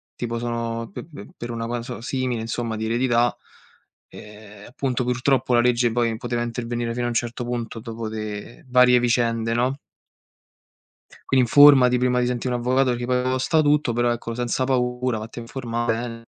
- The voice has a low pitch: Yes, low, 120 Hz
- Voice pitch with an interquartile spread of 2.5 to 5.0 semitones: No, narrow, 1.4 semitones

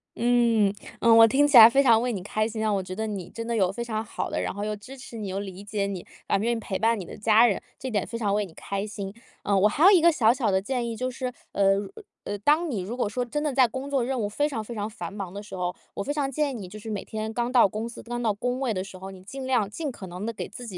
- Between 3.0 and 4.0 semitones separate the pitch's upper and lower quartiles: Yes, average, 3.6 semitones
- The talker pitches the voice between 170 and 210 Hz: No, high, 220 Hz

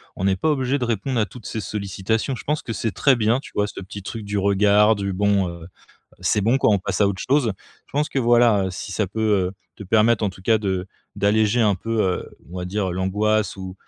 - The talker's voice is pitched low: Yes, low, 105 Hz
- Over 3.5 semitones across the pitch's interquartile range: No, average, 2.9 semitones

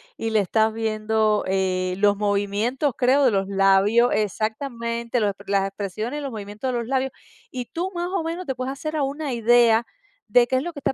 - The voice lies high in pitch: Yes, high, 230 Hz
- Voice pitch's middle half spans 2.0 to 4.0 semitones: No, average, 4.4 semitones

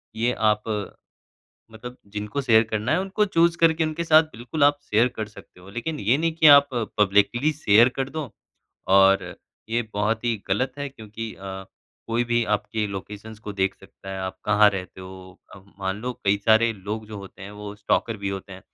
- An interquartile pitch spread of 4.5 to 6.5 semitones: No, average, 3.7 semitones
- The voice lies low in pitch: Yes, low, 110 Hz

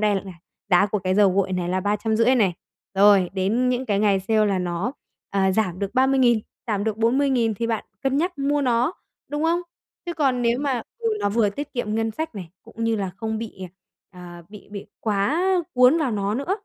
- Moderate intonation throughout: Yes, average, 4.3 semitones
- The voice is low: No, high, 220 Hz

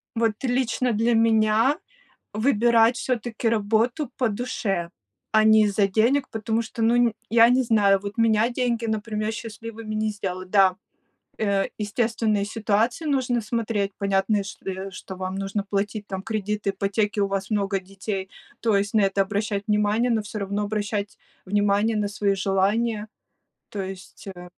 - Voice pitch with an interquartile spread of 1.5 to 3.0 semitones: Yes, narrow, 2.4 semitones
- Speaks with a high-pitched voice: Yes, high, 215 Hz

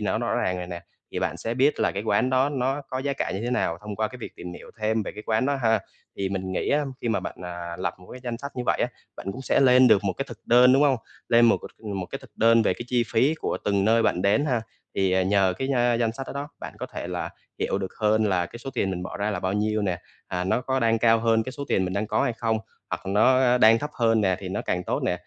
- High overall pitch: No, low, 110 Hz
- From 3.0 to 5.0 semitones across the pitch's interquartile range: Yes, average, 4.5 semitones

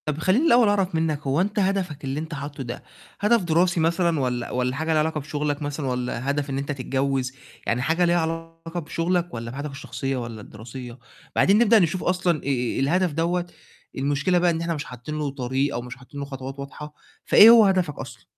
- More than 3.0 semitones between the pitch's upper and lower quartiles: Yes, average, 4.4 semitones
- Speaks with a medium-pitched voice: Yes, medium, 150 Hz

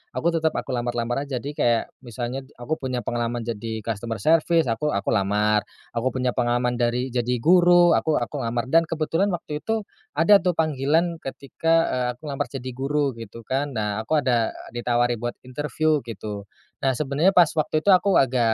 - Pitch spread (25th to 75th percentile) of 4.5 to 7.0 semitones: Yes, average, 4.8 semitones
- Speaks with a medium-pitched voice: No, low, 130 Hz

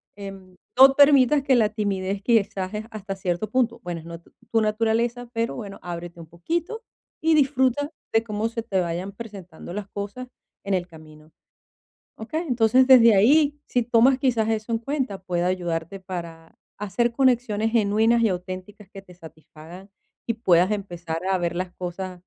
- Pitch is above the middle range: Yes, high, 210 Hz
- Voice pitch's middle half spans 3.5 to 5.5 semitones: Yes, average, 4.6 semitones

